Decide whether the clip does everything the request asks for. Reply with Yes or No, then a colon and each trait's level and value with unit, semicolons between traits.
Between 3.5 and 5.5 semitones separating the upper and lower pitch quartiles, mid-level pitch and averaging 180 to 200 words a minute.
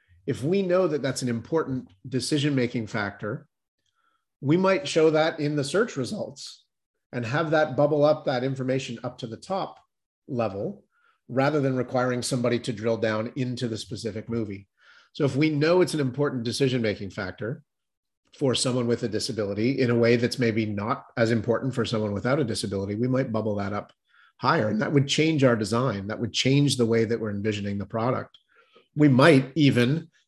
No: average, 4.2 semitones; low, 125 Hz; average, 185 wpm